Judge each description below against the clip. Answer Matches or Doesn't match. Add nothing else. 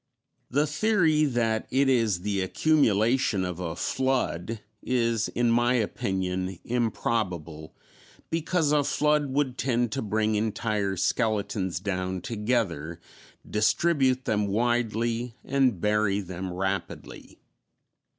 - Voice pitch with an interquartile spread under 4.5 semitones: Doesn't match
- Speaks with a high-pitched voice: Doesn't match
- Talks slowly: Matches